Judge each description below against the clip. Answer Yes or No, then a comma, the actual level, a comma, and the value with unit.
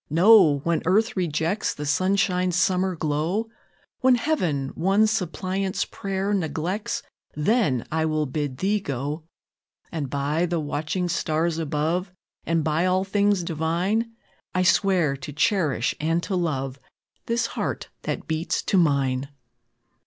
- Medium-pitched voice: Yes, medium, 170 Hz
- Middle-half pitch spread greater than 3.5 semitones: Yes, average, 4.3 semitones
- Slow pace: Yes, slow, 130 wpm